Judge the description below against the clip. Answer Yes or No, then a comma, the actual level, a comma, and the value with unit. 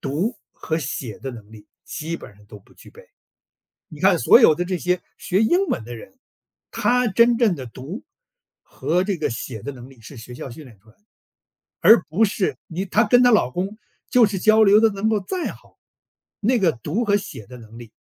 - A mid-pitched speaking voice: Yes, medium, 180 Hz